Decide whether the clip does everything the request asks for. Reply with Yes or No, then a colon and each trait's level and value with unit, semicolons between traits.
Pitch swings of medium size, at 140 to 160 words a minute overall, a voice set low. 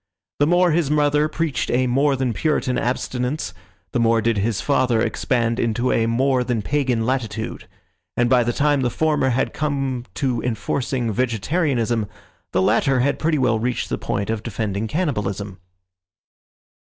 Yes: average, 3.6 semitones; average, 155 wpm; low, 125 Hz